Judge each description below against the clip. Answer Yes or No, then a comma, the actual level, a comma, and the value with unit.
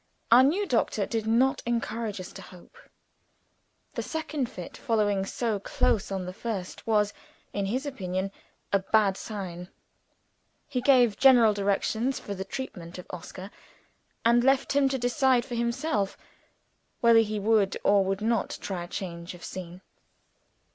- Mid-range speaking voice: No, high, 215 Hz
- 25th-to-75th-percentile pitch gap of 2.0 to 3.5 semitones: No, average, 4.0 semitones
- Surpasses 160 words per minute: No, average, 150 wpm